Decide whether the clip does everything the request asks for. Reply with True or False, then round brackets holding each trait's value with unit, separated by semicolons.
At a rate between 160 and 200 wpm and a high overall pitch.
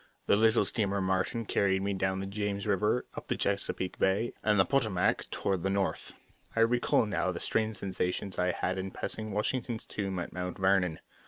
False (185 wpm; 100 Hz)